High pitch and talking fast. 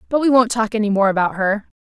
Yes: high, 220 Hz; fast, 265 wpm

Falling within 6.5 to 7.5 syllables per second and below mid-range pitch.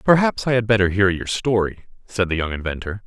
No: 5.8 syllables/s; low, 105 Hz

